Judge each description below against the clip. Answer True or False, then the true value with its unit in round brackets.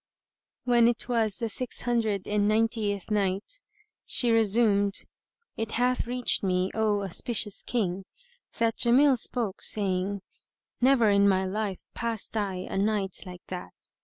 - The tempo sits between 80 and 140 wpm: True (135 wpm)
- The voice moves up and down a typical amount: True (3.1 semitones)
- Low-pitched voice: False (215 Hz)